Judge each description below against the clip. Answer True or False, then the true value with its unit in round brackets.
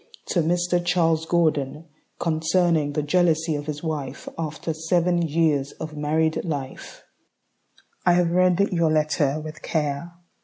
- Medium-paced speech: False (130 wpm)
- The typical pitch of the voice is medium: True (160 Hz)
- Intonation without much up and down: True (2.3 semitones)